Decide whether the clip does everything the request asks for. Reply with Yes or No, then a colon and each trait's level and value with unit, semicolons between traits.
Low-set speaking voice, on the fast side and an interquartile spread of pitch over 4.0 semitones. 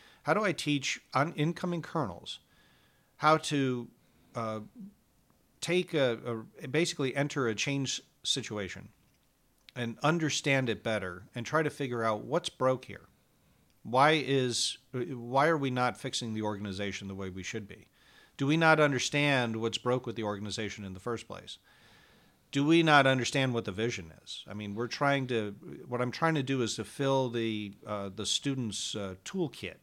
No: low, 125 Hz; average, 170 wpm; average, 4.9 semitones